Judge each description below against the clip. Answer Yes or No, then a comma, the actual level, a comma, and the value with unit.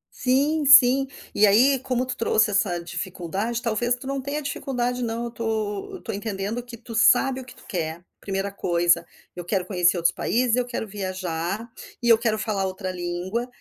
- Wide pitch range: No, average, 4.8 semitones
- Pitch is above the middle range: Yes, high, 220 Hz